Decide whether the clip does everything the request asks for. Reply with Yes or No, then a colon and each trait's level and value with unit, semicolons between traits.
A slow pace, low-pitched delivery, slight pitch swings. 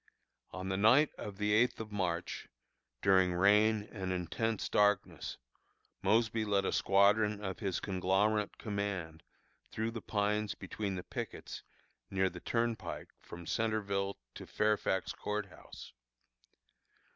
Yes: slow, 125 wpm; low, 100 Hz; narrow, 2.1 semitones